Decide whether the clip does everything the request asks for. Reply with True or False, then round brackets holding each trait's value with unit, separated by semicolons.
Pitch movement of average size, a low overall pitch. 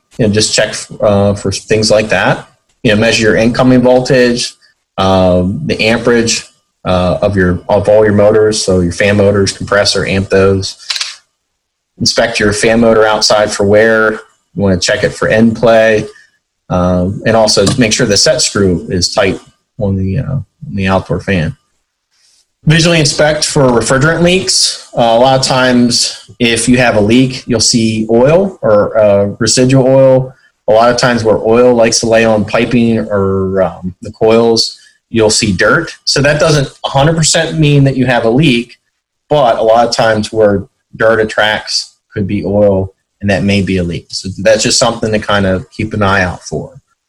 True (3.6 semitones; 110 Hz)